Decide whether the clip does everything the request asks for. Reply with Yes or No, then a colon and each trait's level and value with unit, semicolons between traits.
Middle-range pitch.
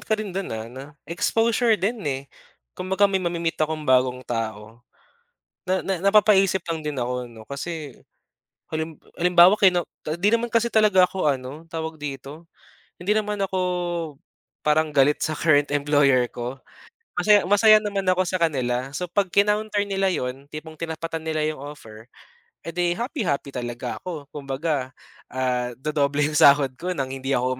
Yes: medium, 160 Hz